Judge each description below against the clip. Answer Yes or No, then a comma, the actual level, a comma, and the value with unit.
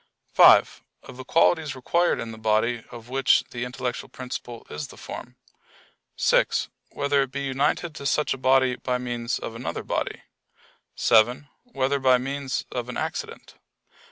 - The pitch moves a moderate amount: No, narrow, 2.3 semitones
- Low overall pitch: Yes, low, 130 Hz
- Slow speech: No, average, 155 wpm